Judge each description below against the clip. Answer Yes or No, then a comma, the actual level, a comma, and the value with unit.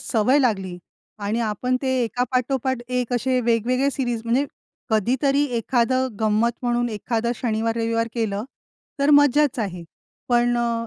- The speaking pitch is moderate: No, high, 240 Hz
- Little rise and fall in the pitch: Yes, narrow, 2.2 semitones